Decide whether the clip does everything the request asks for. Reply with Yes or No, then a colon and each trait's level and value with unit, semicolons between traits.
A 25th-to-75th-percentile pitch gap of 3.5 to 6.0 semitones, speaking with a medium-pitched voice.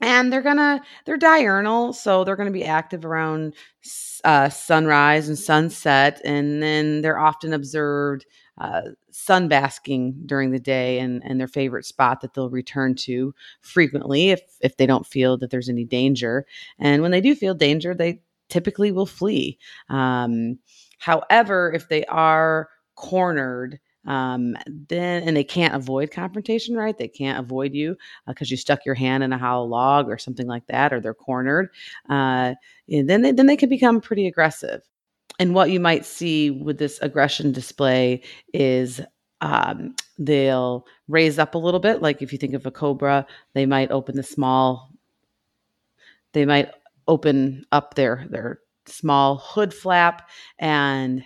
Yes: average, 4.5 semitones; medium, 145 Hz